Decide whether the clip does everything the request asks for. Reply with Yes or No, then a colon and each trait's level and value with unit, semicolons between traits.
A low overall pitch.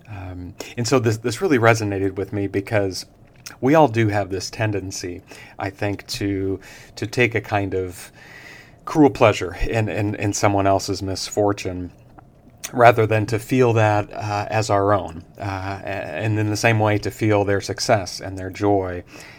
Yes: low, 105 Hz